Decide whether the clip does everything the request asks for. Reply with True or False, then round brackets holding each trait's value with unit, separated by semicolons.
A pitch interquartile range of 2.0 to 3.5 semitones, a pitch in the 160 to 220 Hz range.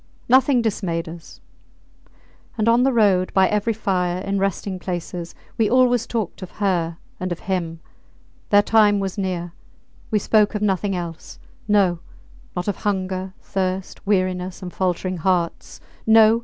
True (2.7 semitones; 190 Hz)